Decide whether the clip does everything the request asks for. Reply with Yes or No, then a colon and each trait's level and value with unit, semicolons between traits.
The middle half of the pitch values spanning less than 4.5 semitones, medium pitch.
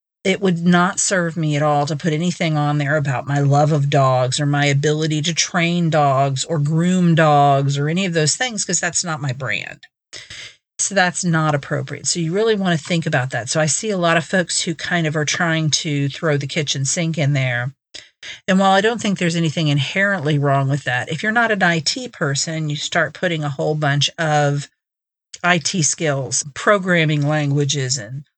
Yes: average, 3.4 semitones; medium, 155 Hz